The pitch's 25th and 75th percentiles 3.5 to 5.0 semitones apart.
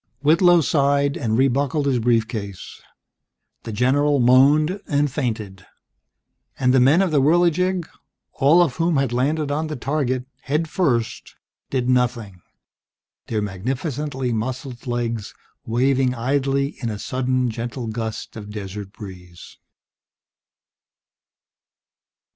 Yes: average, 4.0 semitones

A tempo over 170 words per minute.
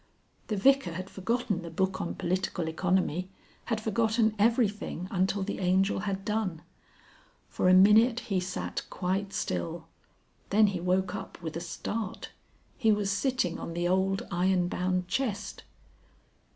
No: average, 145 wpm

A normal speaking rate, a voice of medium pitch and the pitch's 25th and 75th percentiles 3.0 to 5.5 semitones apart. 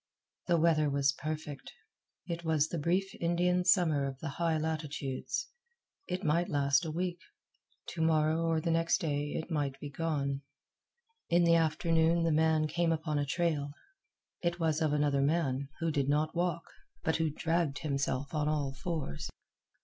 No: average, 160 wpm; medium, 160 Hz; narrow, 2.6 semitones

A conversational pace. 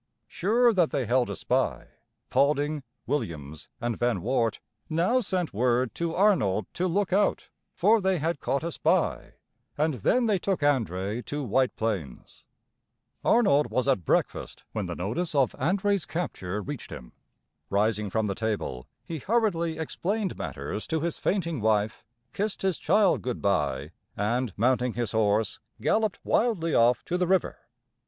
Yes: average, 155 wpm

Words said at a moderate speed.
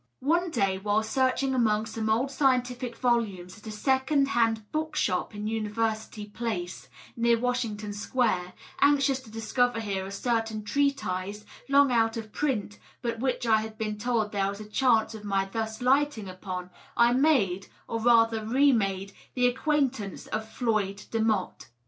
Yes: average, 155 wpm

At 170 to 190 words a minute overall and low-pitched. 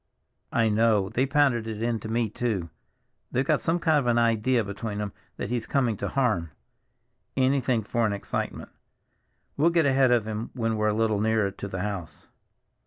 Yes: average, 180 wpm; low, 115 Hz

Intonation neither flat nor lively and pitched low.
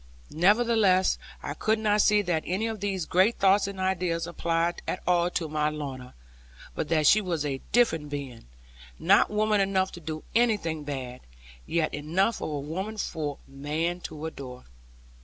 No: average, 4.8 semitones; medium, 170 Hz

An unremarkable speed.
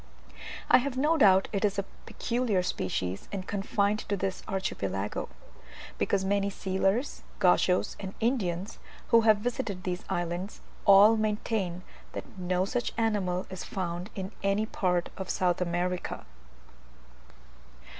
No: slow, 130 wpm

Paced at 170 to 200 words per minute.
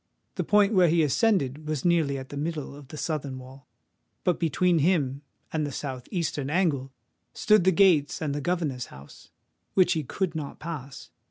Yes: average, 180 wpm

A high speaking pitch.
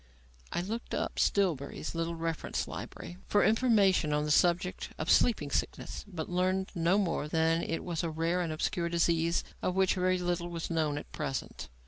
No: medium, 170 Hz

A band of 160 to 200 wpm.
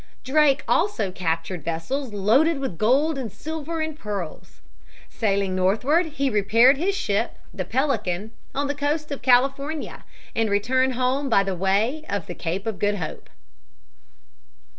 No: average, 145 wpm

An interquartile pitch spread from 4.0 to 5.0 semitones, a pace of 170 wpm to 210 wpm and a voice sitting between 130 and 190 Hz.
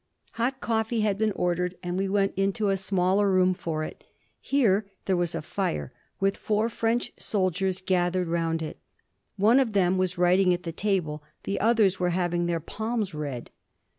No: average, 2.9 semitones; average, 175 wpm; medium, 185 Hz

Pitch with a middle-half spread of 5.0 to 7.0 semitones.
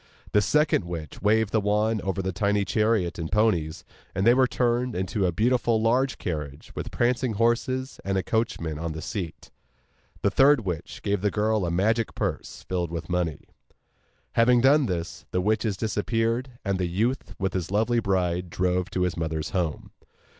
No: average, 4.4 semitones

